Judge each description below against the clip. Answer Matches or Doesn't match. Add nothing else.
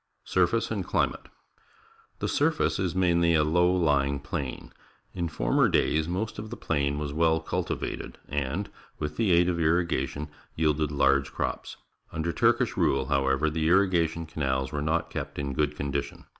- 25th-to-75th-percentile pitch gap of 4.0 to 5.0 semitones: Doesn't match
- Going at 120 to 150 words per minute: Doesn't match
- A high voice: Doesn't match